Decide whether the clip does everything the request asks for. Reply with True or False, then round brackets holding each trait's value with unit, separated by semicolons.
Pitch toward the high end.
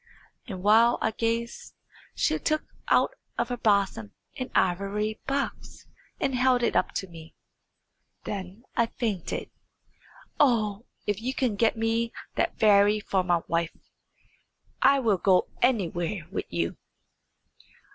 True (215 Hz)